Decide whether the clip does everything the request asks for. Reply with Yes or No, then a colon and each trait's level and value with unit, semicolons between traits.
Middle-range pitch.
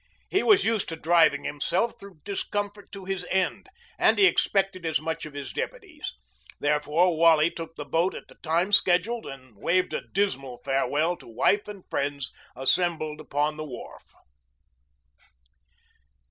Yes: medium, 165 Hz